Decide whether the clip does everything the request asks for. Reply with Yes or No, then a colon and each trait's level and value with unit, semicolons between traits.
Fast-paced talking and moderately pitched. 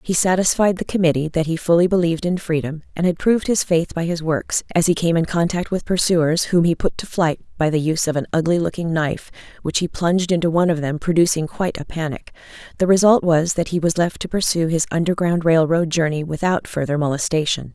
Yes: fast, 225 wpm; medium, 170 Hz